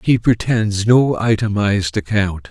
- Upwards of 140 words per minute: No, slow, 120 wpm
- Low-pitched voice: Yes, low, 105 Hz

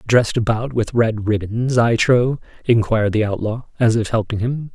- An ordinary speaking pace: Yes, average, 175 wpm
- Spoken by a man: Yes, male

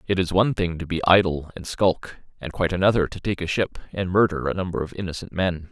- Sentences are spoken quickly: Yes, fast, 240 wpm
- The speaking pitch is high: No, very low, 90 Hz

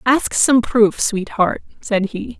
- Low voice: No, high, 220 Hz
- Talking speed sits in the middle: Yes, average, 150 wpm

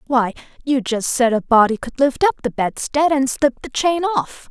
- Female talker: Yes, female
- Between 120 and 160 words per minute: No, fast, 215 wpm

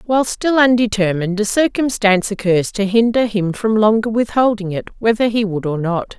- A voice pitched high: Yes, high, 215 Hz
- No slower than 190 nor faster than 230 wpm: No, average, 175 wpm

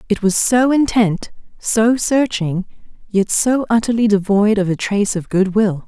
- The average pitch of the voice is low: No, high, 210 Hz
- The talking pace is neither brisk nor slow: Yes, average, 165 wpm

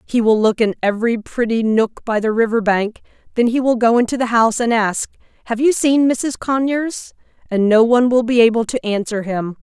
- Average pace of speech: No, fast, 210 wpm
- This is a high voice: Yes, high, 230 Hz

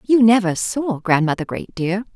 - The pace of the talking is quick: No, average, 165 wpm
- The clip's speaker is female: Yes, female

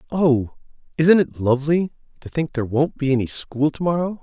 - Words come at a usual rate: Yes, average, 185 wpm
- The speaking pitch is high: No, medium, 150 Hz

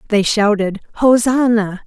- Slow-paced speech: Yes, slow, 95 wpm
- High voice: Yes, high, 215 Hz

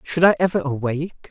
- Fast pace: No, average, 185 wpm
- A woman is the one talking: No, male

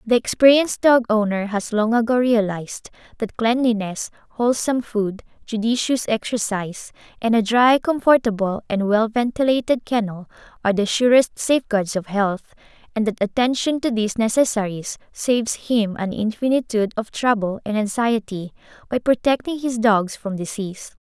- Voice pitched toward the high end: Yes, high, 225 Hz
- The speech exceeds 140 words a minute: No, slow, 135 wpm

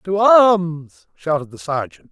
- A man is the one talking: Yes, male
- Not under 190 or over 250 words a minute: No, average, 140 wpm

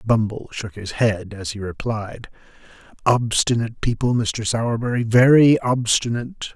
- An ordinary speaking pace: No, slow, 120 wpm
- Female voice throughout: No, male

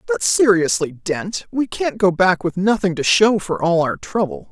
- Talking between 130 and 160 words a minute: No, average, 200 wpm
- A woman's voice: Yes, female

